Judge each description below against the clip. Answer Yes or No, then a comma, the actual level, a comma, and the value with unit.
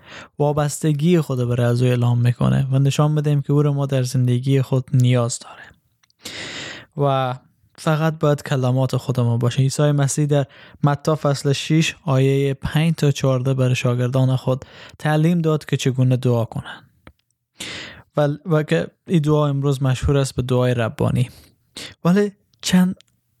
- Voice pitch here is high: No, low, 135 Hz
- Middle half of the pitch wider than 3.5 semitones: No, average, 3.0 semitones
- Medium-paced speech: Yes, average, 145 wpm